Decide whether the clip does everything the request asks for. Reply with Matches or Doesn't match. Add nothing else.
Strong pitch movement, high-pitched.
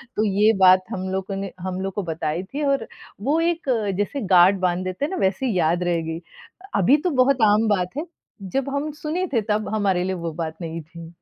Matches